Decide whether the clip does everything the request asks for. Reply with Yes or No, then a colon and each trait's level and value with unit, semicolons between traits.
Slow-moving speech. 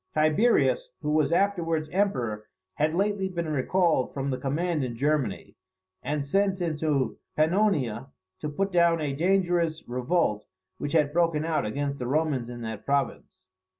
No: average, 150 wpm